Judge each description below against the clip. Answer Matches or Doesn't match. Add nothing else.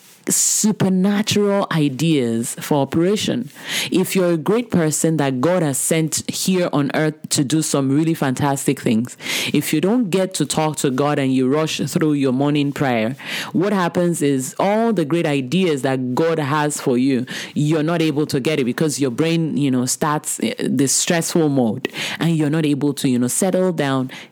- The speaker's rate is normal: Matches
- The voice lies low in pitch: Doesn't match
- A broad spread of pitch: Doesn't match